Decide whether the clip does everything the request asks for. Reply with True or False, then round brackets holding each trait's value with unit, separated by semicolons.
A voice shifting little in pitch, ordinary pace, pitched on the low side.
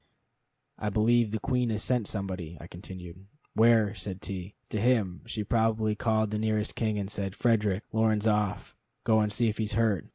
True (2.1 semitones; 175 wpm; 105 Hz)